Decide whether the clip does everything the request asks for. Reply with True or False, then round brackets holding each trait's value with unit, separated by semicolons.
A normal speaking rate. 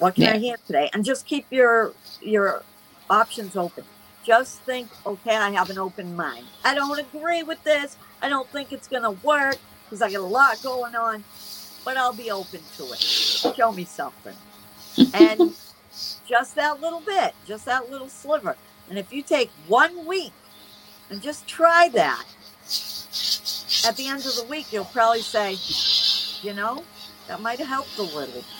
True (175 wpm)